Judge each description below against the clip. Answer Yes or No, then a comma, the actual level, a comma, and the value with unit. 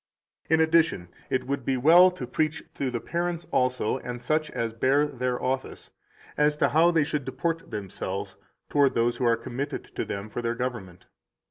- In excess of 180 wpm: Yes, average, 190 wpm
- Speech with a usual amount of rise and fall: Yes, average, 4.5 semitones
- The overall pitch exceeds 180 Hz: No, low, 130 Hz